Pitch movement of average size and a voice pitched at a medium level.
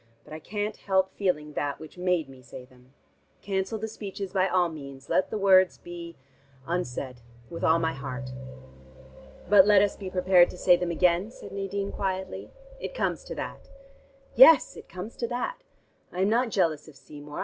Yes: average, 4.2 semitones; medium, 180 Hz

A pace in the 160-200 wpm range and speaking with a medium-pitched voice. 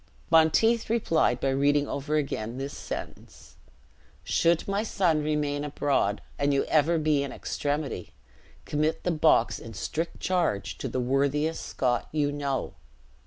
No: average, 140 wpm; medium, 145 Hz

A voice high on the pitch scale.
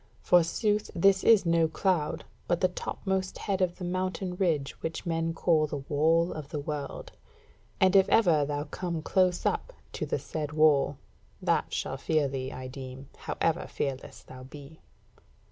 No: medium, 165 Hz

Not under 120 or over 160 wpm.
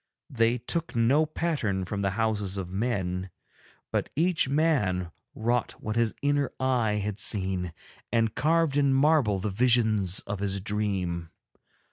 Yes: average, 140 wpm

